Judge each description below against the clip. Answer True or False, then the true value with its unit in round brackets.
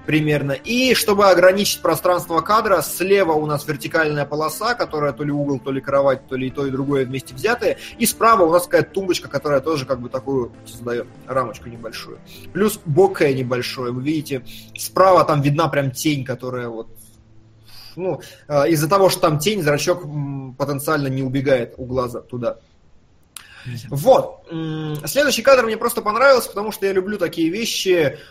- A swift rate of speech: True (165 wpm)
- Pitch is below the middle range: False (150 Hz)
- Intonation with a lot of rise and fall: True (5.7 semitones)